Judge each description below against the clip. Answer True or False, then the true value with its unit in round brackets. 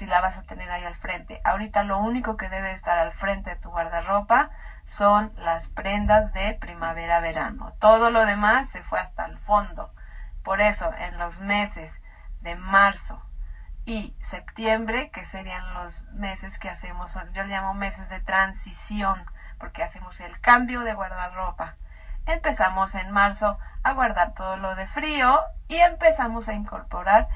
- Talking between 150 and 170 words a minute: True (160 wpm)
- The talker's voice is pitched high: True (195 Hz)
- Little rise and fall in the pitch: False (3.0 semitones)